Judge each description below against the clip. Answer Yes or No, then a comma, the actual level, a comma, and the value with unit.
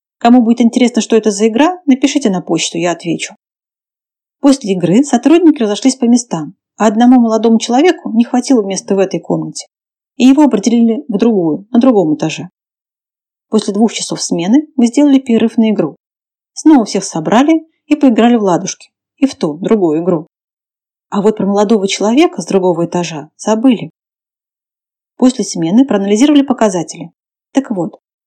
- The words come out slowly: No, average, 155 wpm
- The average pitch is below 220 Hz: No, high, 225 Hz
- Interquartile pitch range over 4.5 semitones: Yes, average, 5.1 semitones